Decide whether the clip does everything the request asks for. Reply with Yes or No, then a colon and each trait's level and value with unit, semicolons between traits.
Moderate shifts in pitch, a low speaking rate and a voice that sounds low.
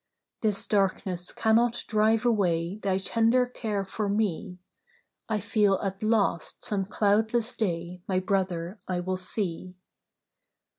No: average, 3.0 semitones; slow, 120 wpm; high, 200 Hz